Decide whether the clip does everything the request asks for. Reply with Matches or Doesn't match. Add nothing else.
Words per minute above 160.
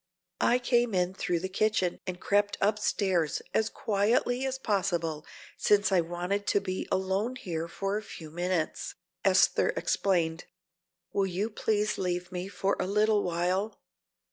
Doesn't match